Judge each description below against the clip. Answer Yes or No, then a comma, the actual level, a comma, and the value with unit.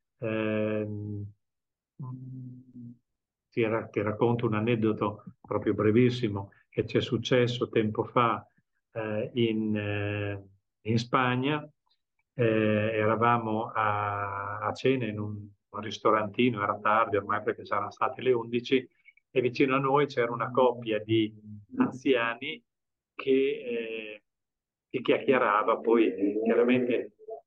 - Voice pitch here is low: Yes, low, 115 Hz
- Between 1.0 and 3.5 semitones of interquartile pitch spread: Yes, average, 2.8 semitones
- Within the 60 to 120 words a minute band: Yes, slow, 115 wpm